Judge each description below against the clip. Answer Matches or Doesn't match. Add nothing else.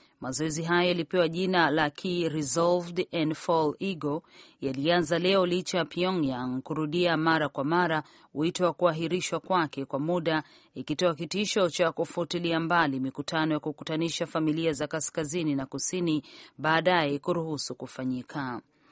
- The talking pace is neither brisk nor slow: Matches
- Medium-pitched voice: Matches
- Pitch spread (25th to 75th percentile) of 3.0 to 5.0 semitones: Doesn't match